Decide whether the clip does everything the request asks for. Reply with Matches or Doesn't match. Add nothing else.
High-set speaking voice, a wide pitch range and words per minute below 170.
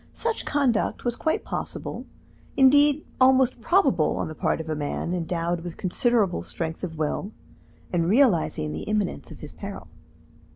Matches